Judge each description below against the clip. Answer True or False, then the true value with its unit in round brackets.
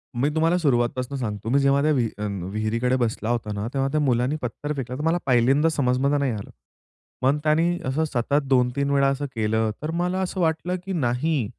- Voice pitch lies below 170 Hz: True (135 Hz)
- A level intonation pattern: False (4.1 semitones)